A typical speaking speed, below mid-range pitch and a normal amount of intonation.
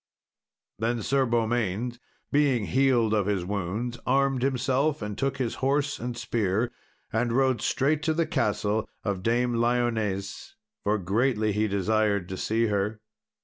Yes: average, 145 wpm; low, 115 Hz; average, 3.8 semitones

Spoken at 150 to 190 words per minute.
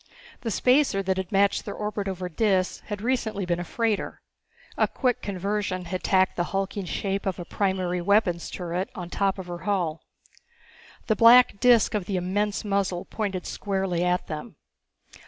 Yes: average, 170 wpm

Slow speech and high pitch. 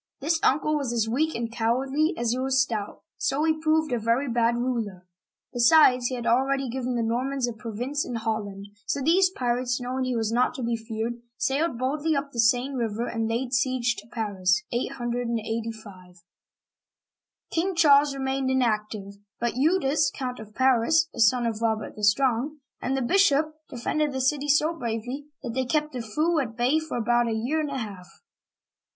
No: average, 185 wpm; high, 245 Hz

